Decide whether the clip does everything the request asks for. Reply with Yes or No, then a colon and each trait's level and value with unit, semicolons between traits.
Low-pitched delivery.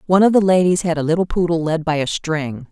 No: medium, 170 Hz